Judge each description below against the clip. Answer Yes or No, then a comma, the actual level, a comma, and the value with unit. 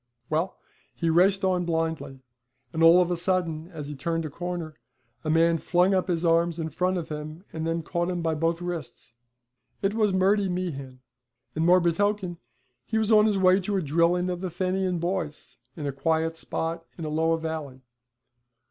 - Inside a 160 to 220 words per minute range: Yes, average, 185 wpm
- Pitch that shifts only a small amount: Yes, narrow, 2.3 semitones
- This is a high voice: No, medium, 170 Hz